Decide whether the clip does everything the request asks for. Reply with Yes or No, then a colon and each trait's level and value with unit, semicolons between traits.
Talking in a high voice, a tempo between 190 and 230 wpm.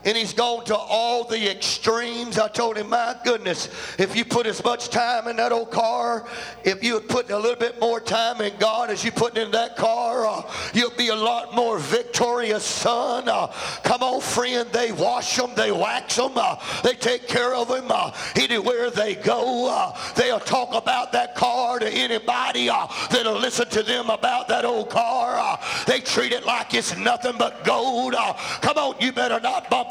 Yes: high, 235 Hz; average, 200 wpm